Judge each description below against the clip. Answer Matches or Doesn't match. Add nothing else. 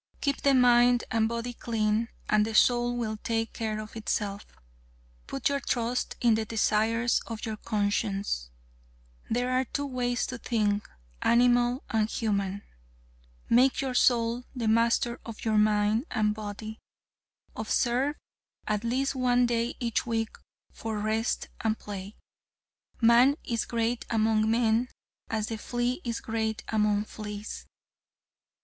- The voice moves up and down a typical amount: Doesn't match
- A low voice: Doesn't match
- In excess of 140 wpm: Doesn't match